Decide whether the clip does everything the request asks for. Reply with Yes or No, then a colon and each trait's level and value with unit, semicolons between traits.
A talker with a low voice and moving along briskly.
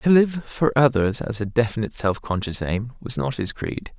Yes: low, 120 Hz; fast, 210 wpm